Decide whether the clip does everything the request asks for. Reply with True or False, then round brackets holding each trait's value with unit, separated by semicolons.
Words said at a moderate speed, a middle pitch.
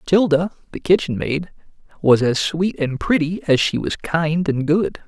True (175 wpm; 160 Hz)